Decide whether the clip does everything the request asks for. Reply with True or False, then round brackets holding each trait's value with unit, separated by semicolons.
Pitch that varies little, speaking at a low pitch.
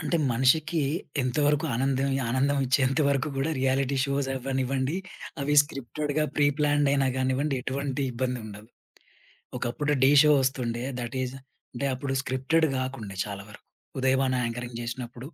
True (2.0 semitones; 130 Hz)